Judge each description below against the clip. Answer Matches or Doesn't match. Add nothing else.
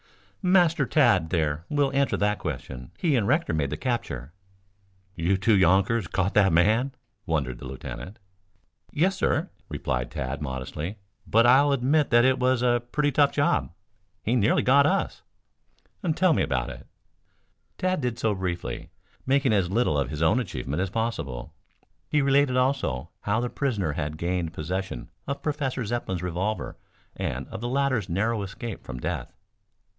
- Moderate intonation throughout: Doesn't match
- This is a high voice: Doesn't match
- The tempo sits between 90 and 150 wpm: Doesn't match